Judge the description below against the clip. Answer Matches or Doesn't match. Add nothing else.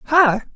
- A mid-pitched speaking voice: Doesn't match